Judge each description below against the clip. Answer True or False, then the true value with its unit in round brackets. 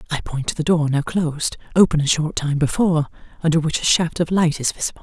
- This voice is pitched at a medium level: True (160 Hz)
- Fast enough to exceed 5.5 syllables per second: True (6.4 syllables/s)